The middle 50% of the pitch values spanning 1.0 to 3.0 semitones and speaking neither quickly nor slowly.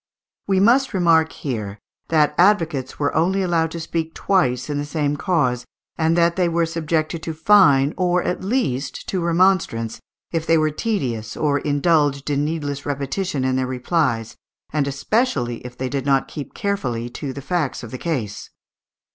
No: average, 4.1 semitones; average, 170 wpm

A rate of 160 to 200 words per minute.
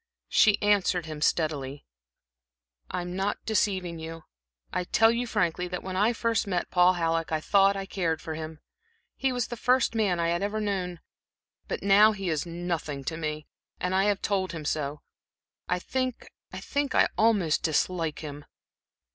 Yes: average, 165 wpm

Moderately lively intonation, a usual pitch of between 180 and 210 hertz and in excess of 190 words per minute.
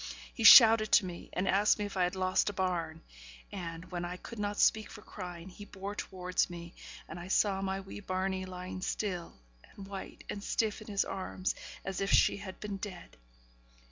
No: narrow, 2.1 semitones; high, 190 Hz; average, 200 wpm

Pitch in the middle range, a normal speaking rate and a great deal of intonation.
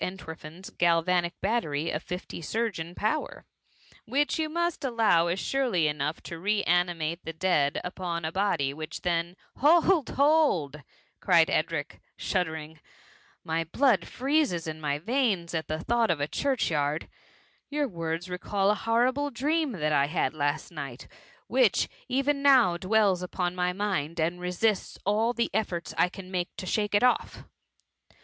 Yes: medium, 180 Hz; average, 165 wpm; wide, 6.3 semitones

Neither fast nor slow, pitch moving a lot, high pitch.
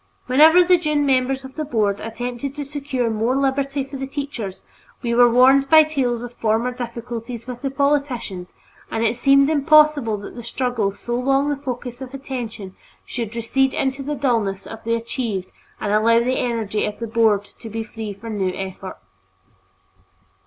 No: average, 175 wpm; average, 3.5 semitones; high, 245 Hz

